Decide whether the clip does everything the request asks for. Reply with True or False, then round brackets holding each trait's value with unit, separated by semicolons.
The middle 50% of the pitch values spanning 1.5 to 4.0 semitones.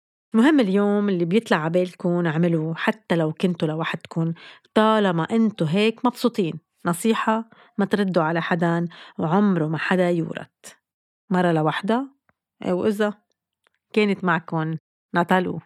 False (4.5 semitones)